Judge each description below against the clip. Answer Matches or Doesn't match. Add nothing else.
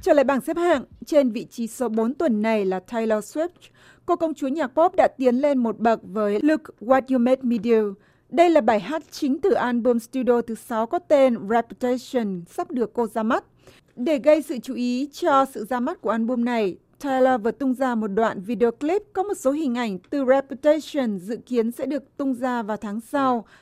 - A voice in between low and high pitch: Doesn't match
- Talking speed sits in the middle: Matches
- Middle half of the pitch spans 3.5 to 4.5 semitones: Matches